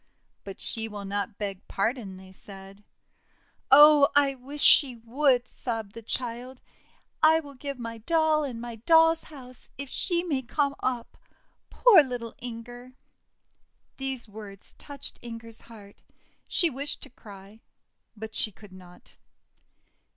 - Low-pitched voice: No, high, 240 Hz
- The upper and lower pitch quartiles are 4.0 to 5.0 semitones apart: Yes, average, 4.6 semitones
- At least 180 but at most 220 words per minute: No, slow, 135 wpm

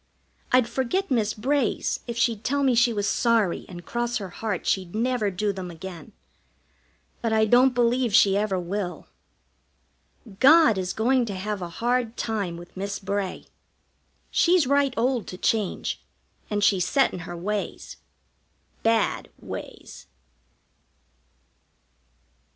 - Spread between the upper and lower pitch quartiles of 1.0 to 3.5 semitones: No, average, 4.2 semitones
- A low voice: No, high, 220 Hz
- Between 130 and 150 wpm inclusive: Yes, slow, 135 wpm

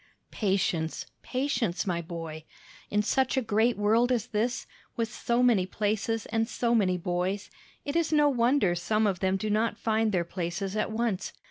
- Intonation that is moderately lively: Yes, average, 4.1 semitones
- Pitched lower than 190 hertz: No, high, 215 Hz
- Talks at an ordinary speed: Yes, average, 175 wpm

